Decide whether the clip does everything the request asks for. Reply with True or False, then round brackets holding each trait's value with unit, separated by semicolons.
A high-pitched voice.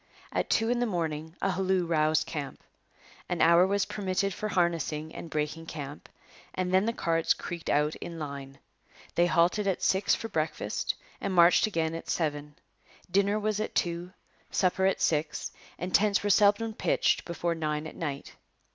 False (170 Hz)